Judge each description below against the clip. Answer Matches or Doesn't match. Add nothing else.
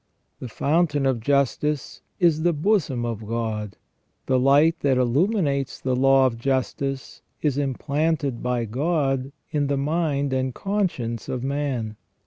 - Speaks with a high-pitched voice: Doesn't match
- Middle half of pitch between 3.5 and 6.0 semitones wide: Doesn't match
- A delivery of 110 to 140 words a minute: Matches